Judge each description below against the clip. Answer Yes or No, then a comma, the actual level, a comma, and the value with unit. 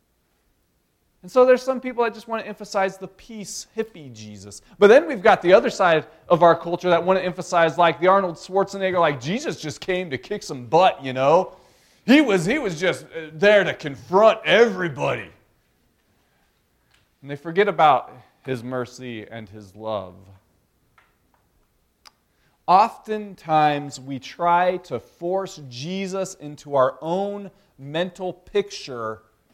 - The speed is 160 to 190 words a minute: No, average, 145 wpm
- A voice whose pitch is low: No, medium, 170 Hz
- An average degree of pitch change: No, wide, 6.8 semitones